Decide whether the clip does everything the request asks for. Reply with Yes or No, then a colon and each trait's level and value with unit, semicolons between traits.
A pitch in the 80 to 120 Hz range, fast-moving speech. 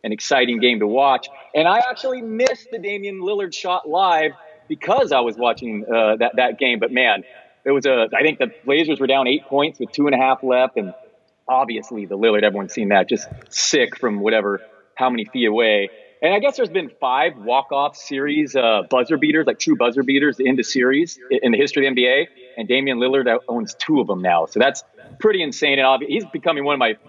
No: medium, 140 Hz; fast, 220 wpm